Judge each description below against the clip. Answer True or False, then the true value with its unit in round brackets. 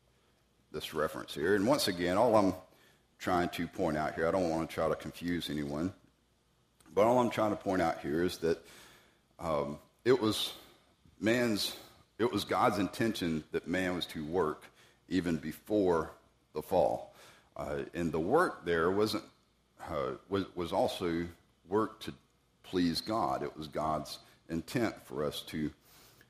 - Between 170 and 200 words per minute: False (155 wpm)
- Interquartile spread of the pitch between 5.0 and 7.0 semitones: False (4.6 semitones)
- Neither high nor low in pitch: False (85 Hz)